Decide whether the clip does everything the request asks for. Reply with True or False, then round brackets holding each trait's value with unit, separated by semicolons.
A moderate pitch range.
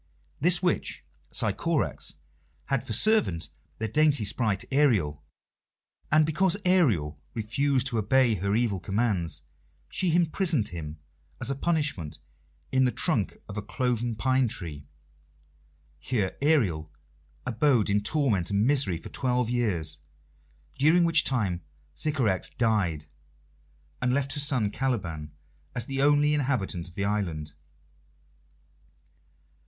False (6.7 semitones)